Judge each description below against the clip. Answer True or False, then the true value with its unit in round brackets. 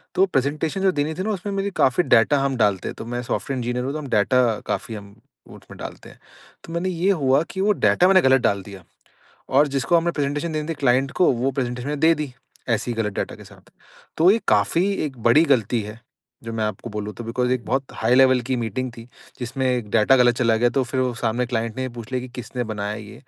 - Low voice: True (130 Hz)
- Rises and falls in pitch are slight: False (4.2 semitones)